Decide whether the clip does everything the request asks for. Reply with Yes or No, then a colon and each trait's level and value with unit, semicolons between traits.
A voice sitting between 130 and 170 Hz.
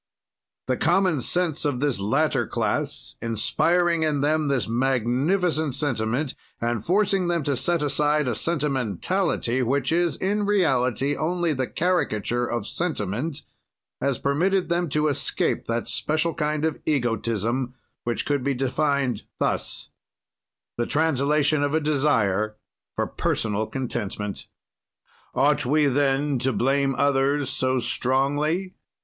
Yes: medium, 140 Hz